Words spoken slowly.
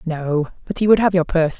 No: fast, 265 wpm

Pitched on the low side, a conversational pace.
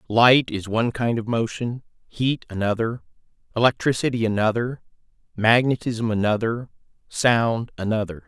No: low, 115 Hz; slow, 100 wpm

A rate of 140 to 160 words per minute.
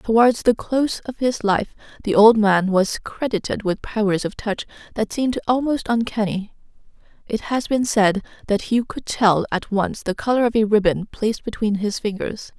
No: average, 180 wpm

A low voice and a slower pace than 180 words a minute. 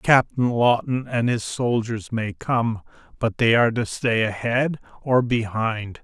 Yes: low, 120 Hz; average, 150 wpm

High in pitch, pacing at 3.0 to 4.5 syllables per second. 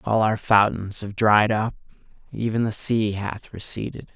No: low, 105 Hz; 4.3 syllables/s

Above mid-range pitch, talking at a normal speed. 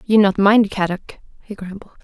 Yes: high, 200 Hz; average, 175 wpm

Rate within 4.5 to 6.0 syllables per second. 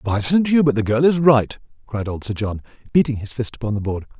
Yes: 5.7 syllables/s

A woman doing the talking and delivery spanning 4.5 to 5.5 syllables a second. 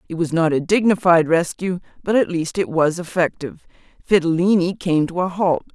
Yes: female; 5.4 syllables/s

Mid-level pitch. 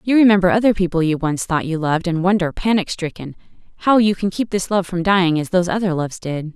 Yes: medium, 180 Hz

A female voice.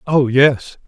No: male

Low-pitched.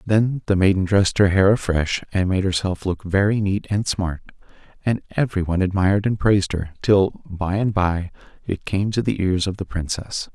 Yes: very low, 95 Hz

